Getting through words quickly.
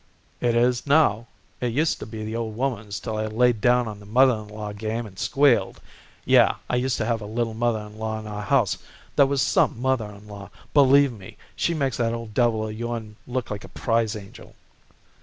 Yes: fast, 215 wpm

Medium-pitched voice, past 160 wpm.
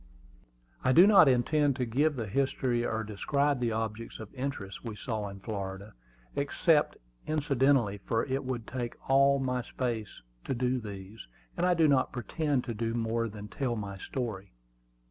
No: low, 120 Hz; average, 170 wpm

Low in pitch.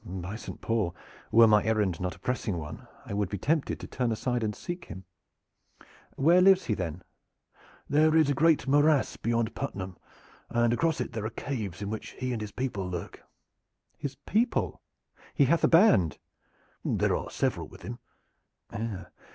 Yes: low, 115 Hz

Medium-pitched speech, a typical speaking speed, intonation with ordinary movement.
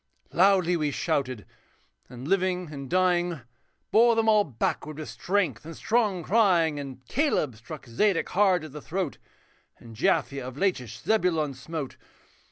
No: medium, 165 Hz; average, 145 wpm; wide, 5.7 semitones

